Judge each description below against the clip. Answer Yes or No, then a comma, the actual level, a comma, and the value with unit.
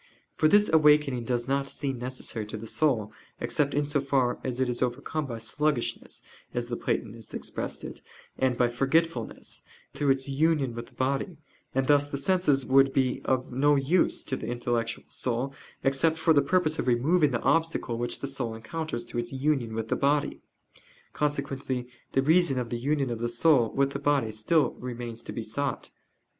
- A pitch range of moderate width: Yes, average, 3.5 semitones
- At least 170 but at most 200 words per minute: Yes, average, 185 wpm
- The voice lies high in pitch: No, low, 135 Hz